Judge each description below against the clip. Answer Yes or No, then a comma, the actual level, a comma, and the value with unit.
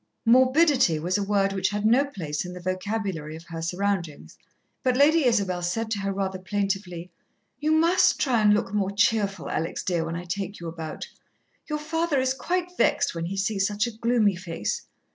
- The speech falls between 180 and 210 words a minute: Yes, average, 190 wpm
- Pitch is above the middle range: Yes, high, 200 Hz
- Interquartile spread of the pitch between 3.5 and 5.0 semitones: No, wide, 5.4 semitones